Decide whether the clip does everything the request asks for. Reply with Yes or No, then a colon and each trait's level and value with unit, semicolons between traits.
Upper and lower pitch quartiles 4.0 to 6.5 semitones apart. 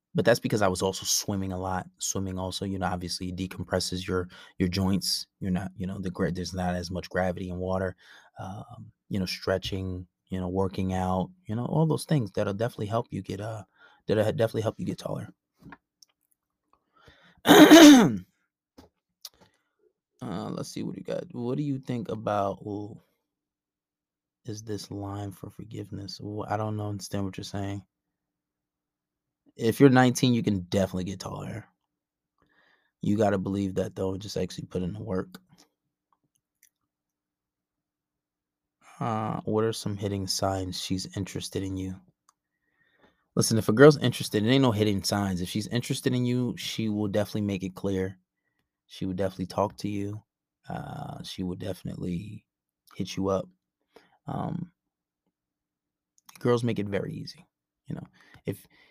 No: average, 2.9 semitones